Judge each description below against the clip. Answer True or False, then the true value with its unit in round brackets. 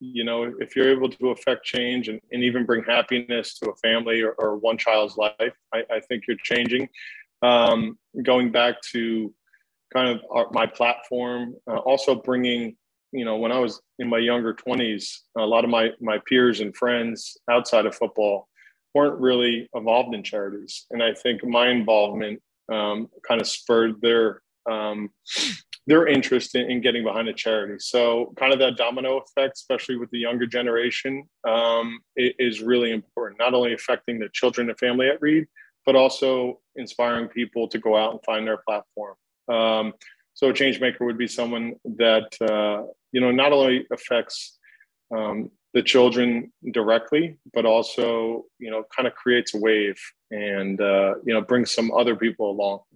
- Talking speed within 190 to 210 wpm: False (175 wpm)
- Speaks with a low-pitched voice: True (120 Hz)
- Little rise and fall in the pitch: True (1.8 semitones)